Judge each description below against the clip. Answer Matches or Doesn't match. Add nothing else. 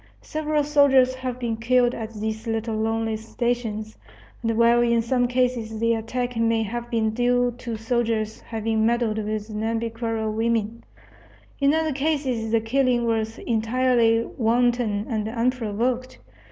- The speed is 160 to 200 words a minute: Doesn't match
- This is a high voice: Matches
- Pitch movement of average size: Doesn't match